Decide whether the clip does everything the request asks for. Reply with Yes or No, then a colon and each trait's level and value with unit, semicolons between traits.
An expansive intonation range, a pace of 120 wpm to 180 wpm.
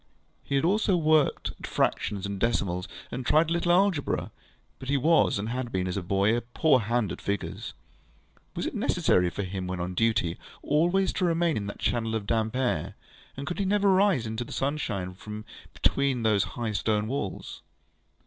No: wide, 7.5 semitones; average, 190 wpm